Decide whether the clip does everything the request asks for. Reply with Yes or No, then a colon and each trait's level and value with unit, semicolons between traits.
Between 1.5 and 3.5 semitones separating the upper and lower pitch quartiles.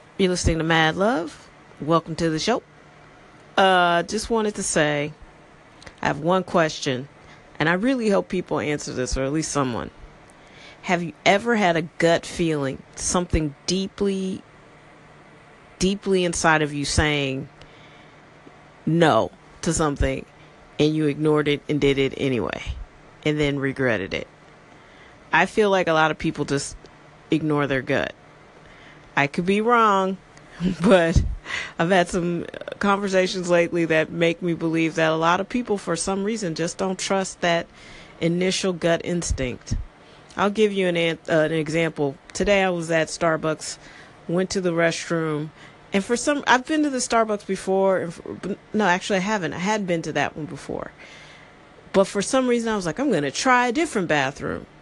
No: average, 4.2 semitones